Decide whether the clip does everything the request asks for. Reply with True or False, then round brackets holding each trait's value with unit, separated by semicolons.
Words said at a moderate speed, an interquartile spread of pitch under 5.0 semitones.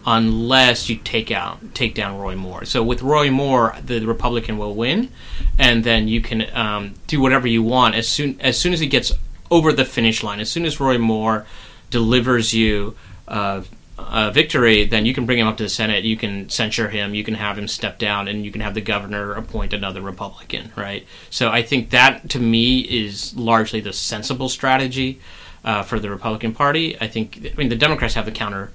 False (210 wpm; 3.1 semitones)